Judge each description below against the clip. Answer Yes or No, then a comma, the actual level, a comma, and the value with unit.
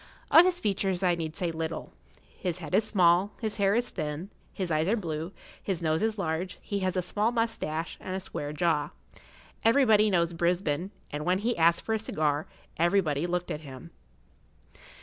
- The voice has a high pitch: No, medium, 180 Hz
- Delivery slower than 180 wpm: No, average, 185 wpm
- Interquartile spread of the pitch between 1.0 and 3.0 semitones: No, average, 4.2 semitones